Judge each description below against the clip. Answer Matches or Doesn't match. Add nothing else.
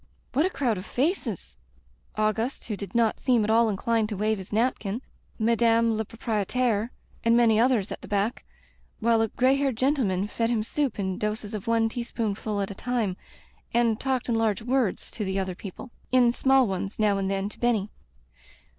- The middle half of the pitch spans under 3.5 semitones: Matches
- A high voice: Matches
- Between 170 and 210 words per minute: Matches